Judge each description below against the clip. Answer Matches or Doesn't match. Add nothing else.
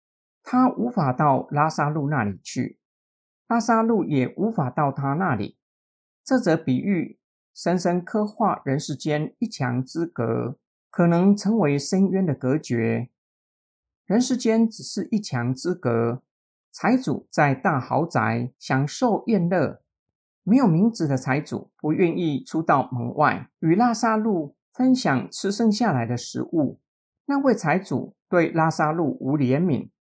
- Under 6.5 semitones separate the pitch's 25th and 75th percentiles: Doesn't match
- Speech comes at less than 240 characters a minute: Matches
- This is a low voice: Doesn't match